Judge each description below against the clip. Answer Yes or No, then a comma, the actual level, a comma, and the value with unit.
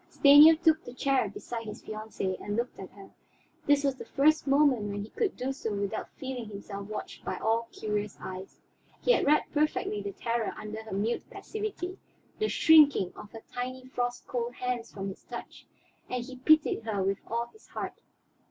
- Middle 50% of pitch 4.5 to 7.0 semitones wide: Yes, average, 5.1 semitones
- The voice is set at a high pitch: Yes, high, 240 Hz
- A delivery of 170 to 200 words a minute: Yes, average, 190 wpm